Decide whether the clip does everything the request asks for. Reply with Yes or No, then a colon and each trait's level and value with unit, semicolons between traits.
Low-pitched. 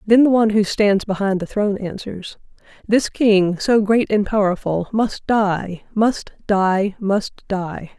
No: high, 200 Hz